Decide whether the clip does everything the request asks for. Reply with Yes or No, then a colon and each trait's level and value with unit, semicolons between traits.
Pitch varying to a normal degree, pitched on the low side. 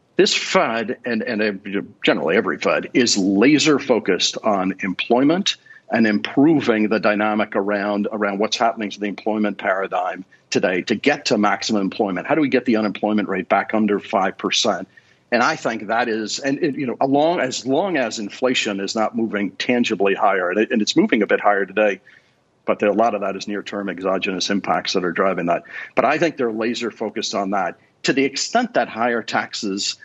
No: narrow, 2.2 semitones; low, 105 Hz